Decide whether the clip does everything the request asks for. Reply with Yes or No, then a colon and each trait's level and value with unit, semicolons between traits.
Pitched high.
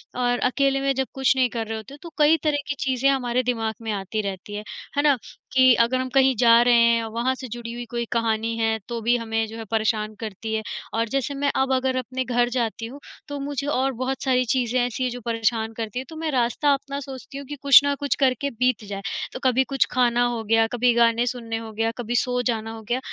Yes: high, 245 Hz